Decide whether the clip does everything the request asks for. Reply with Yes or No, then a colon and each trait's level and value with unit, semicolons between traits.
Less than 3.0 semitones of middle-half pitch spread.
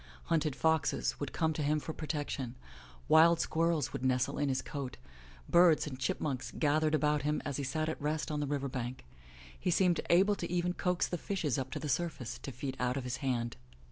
No: average, 3.4 semitones